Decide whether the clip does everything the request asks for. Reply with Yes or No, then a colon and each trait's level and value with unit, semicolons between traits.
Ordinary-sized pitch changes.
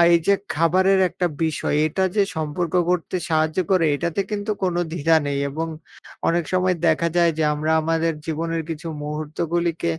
No: narrow, 2.1 semitones